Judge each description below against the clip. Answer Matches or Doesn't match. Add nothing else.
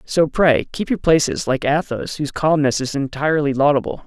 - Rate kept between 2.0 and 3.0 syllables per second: Doesn't match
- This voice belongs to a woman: Doesn't match